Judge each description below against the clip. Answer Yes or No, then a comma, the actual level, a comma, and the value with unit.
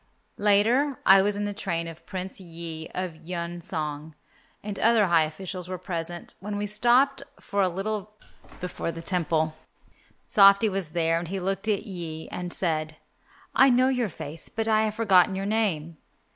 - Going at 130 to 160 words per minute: No, average, 170 wpm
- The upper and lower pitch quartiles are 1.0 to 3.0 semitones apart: No, average, 3.9 semitones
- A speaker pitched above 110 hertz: Yes, medium, 185 Hz